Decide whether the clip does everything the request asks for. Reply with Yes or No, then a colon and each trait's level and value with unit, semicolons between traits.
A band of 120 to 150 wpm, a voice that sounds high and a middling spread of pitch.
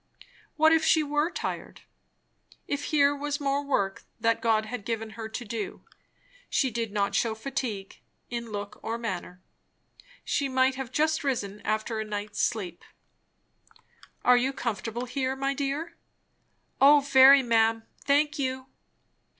Yes: average, 140 wpm; high, 245 Hz; average, 4.3 semitones